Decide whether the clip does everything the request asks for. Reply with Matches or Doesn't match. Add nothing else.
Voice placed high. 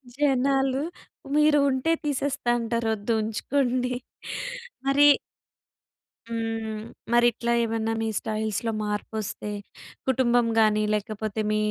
Matches